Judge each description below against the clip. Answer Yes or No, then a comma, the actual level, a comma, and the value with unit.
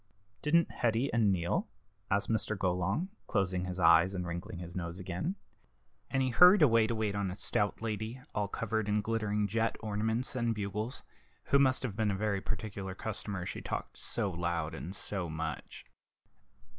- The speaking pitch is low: Yes, low, 105 Hz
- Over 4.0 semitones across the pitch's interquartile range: No, average, 3.5 semitones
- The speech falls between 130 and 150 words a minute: No, average, 170 wpm